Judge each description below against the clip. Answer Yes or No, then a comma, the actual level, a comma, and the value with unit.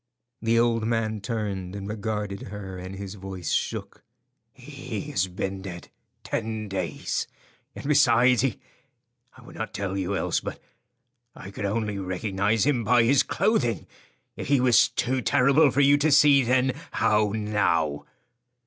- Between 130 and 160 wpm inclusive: Yes, average, 145 wpm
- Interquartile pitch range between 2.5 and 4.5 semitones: Yes, average, 4.1 semitones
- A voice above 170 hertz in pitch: No, low, 110 Hz